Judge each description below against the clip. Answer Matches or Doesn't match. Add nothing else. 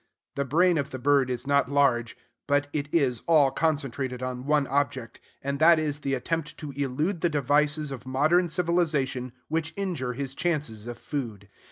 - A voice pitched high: Doesn't match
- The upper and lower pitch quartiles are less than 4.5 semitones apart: Matches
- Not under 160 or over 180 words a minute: Matches